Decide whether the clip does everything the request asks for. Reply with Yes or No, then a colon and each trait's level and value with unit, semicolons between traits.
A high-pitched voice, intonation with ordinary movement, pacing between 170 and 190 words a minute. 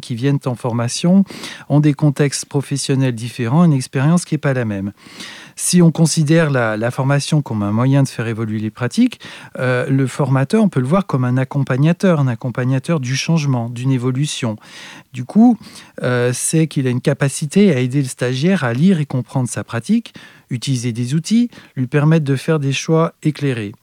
No: medium, 140 Hz; average, 4.4 semitones; average, 185 wpm